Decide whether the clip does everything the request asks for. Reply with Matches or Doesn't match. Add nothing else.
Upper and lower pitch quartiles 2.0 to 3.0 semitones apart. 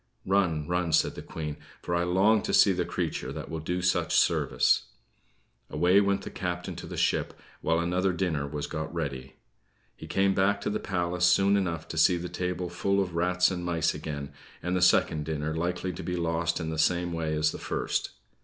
Matches